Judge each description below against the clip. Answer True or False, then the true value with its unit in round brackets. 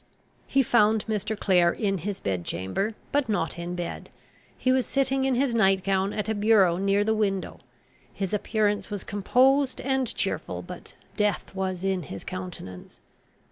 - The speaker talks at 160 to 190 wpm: True (165 wpm)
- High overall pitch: True (205 Hz)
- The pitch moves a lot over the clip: False (3.3 semitones)